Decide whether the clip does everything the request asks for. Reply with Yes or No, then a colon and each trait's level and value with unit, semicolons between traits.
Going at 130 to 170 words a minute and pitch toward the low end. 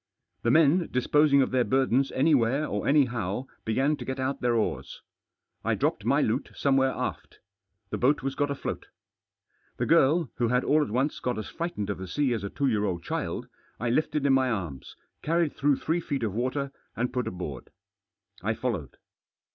No: average, 195 wpm; low, 130 Hz